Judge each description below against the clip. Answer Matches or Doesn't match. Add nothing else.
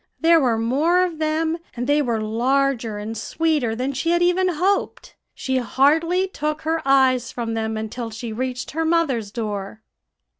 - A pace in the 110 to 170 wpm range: Matches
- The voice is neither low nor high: Doesn't match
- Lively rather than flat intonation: Matches